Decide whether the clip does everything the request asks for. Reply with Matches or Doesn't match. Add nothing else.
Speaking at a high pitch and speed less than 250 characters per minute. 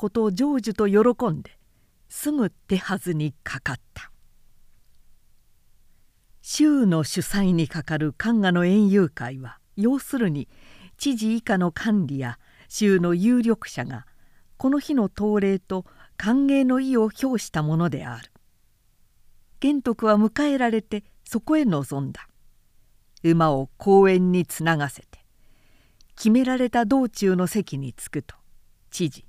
Matches